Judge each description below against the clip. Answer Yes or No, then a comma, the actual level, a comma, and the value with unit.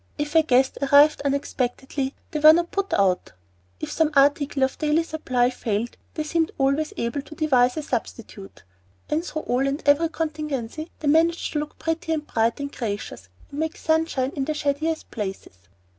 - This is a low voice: No, very high, 290 Hz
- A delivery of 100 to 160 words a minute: No, average, 175 wpm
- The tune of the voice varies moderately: Yes, average, 3.4 semitones